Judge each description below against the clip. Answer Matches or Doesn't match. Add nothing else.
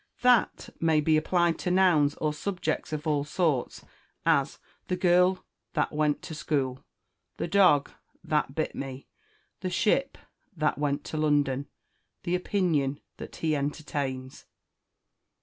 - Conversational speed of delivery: Doesn't match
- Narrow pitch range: Doesn't match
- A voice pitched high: Doesn't match